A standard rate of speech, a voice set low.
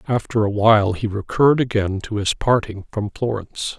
Yes: average, 175 wpm; low, 110 Hz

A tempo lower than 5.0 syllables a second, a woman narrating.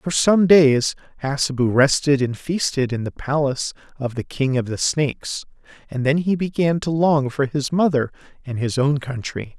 No: 4.7 syllables/s; male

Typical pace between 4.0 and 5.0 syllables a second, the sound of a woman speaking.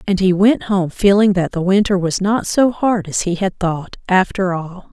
Yes: 4.5 syllables/s; female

